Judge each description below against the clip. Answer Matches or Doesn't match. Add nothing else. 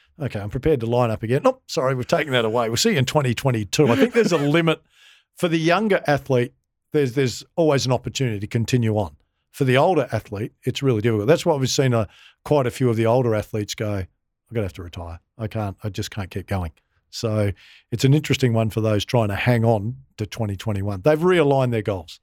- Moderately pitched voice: Doesn't match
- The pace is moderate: Doesn't match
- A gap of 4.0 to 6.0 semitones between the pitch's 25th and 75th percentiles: Matches